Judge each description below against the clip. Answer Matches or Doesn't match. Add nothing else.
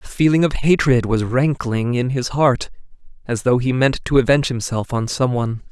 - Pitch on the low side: Matches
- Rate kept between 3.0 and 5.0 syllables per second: Doesn't match